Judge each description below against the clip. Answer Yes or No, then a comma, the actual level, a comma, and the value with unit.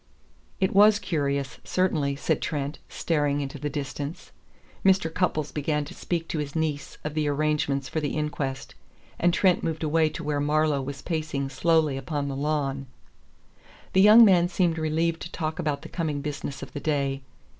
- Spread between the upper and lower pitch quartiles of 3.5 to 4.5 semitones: No, narrow, 2.6 semitones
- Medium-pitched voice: Yes, medium, 150 Hz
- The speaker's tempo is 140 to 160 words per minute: No, average, 175 wpm